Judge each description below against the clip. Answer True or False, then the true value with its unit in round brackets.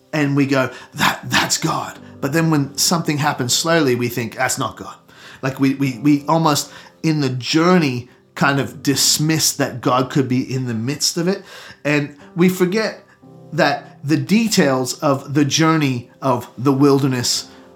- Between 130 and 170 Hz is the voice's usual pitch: True (140 Hz)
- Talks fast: False (165 wpm)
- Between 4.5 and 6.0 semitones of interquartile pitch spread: False (3.4 semitones)